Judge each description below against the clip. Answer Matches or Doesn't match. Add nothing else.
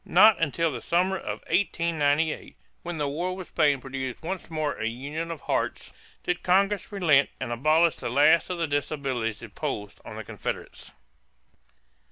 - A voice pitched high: Doesn't match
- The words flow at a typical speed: Matches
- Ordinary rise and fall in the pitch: Matches